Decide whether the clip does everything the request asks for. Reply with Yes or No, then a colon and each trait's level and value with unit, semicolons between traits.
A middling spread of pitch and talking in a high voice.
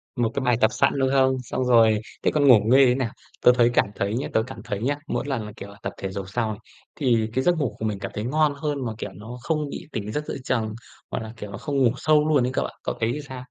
No: average, 4.0 semitones; low, 125 Hz